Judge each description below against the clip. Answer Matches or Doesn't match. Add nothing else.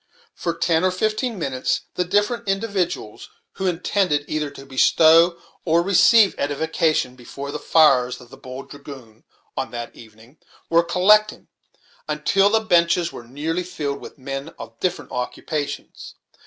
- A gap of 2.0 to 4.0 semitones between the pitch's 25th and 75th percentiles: Doesn't match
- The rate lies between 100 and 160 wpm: Matches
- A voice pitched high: Doesn't match